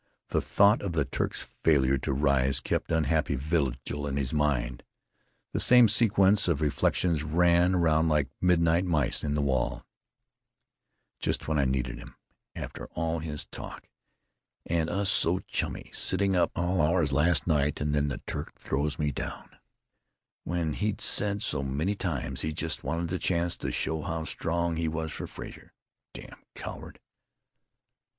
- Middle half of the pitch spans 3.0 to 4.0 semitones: Yes, average, 3.3 semitones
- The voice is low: Yes, very low, 80 Hz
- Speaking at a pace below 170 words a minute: Yes, average, 160 wpm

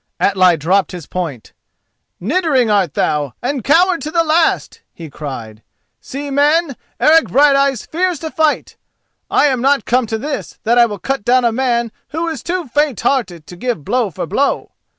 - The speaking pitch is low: No, very high, 255 Hz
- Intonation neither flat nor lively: No, wide, 7.3 semitones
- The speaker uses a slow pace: No, average, 175 wpm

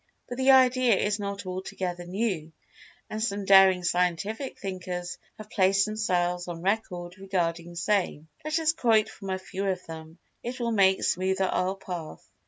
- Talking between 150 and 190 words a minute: Yes, average, 155 wpm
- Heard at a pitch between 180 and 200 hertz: Yes, high, 190 Hz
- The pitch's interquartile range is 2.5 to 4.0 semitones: Yes, average, 3.2 semitones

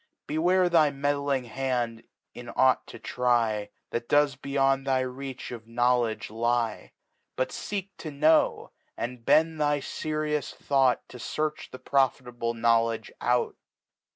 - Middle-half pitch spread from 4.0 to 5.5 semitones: No, average, 3.5 semitones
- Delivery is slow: Yes, slow, 125 wpm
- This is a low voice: Yes, low, 130 Hz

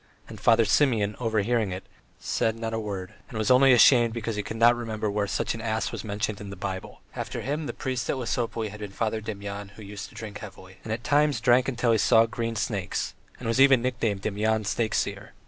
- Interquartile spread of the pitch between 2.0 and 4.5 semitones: Yes, narrow, 2.4 semitones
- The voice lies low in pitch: Yes, low, 110 Hz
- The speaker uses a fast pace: Yes, fast, 220 wpm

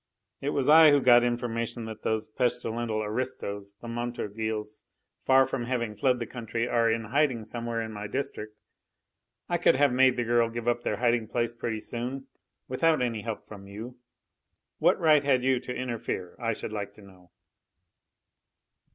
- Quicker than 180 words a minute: No, average, 170 wpm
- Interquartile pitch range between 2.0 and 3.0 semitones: Yes, narrow, 2.4 semitones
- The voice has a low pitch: Yes, low, 120 Hz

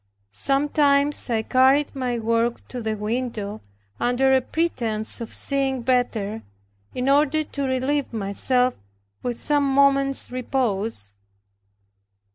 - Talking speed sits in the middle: No, slow, 110 wpm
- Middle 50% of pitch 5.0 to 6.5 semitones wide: No, average, 3.3 semitones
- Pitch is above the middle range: Yes, very high, 255 Hz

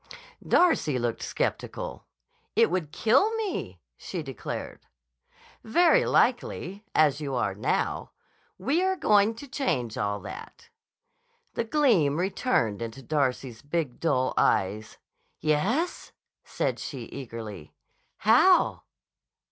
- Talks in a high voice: No, medium, 155 Hz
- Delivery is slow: Yes, slow, 105 wpm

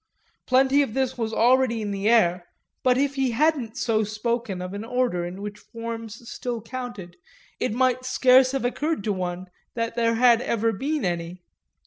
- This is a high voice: Yes, high, 230 Hz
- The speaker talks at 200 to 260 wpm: No, average, 175 wpm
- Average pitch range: Yes, average, 3.7 semitones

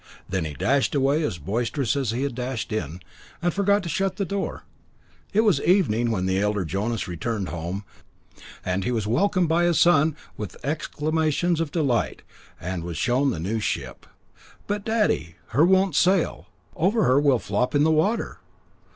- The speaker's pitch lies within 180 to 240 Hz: No, low, 135 Hz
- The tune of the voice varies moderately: No, wide, 8.8 semitones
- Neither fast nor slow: Yes, average, 175 wpm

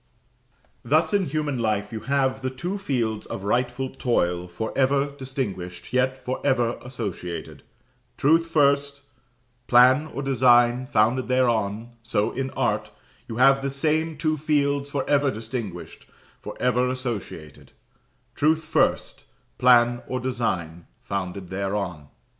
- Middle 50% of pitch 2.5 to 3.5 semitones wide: No, average, 4.0 semitones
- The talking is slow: Yes, slow, 130 wpm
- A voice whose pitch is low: Yes, low, 125 Hz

